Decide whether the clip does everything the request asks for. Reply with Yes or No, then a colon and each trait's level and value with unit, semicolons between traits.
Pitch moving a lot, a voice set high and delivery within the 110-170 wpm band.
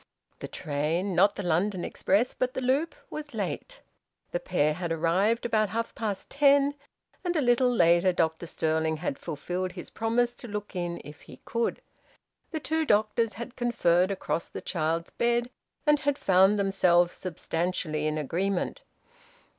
Yes: wide, 5.9 semitones; high, 195 Hz; average, 155 wpm